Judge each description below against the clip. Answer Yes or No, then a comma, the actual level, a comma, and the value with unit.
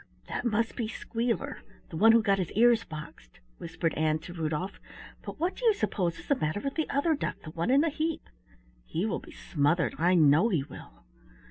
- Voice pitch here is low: No, high, 195 Hz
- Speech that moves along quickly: Yes, fast, 210 wpm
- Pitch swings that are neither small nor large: No, wide, 7.2 semitones